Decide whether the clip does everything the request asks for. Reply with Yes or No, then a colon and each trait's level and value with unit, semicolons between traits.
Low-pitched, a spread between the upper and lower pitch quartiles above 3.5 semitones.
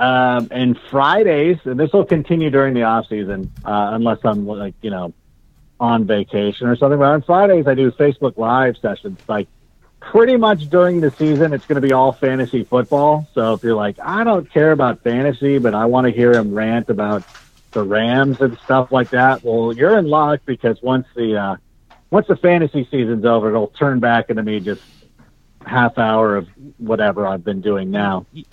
Yes: low, 125 Hz; average, 4.6 semitones